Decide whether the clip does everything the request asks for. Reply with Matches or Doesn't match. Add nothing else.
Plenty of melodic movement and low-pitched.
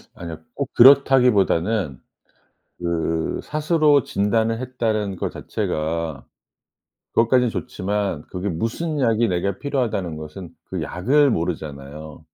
Matches